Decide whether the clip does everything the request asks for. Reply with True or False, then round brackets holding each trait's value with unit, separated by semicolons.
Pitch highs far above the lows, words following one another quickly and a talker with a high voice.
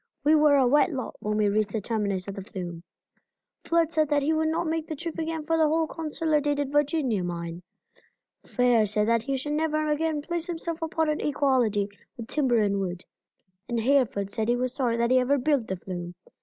True (6.4 semitones; 210 wpm; 270 Hz)